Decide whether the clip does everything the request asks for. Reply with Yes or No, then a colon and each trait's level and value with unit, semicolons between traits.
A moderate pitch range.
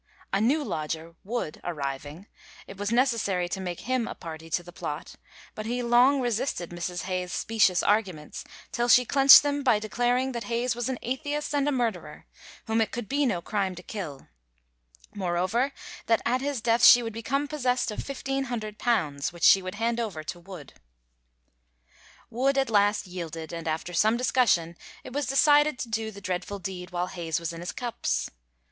No: wide, 5.9 semitones